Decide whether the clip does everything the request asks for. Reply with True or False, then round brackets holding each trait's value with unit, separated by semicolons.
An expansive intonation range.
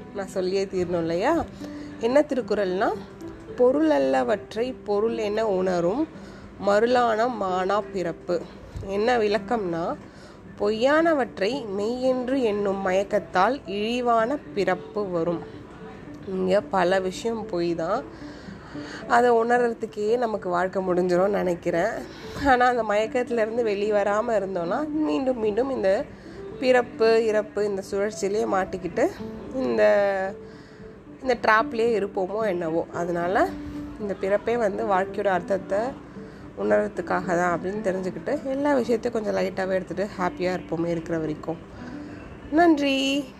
False (4.1 semitones)